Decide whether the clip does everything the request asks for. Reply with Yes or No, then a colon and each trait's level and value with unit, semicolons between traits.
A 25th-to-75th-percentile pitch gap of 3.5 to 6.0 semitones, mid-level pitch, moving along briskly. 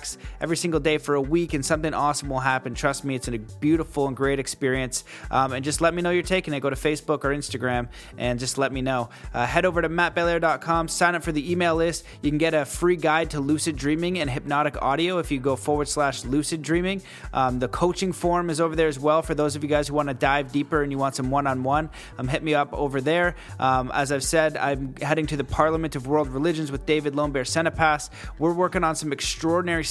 No: average, 3.0 semitones; medium, 150 Hz; fast, 240 wpm